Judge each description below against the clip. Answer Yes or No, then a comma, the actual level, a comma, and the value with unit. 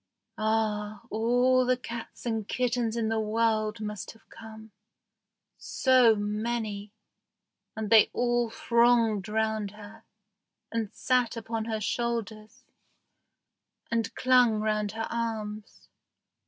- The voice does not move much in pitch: Yes, narrow, 1.7 semitones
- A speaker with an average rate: No, slow, 110 wpm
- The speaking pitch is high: Yes, high, 225 Hz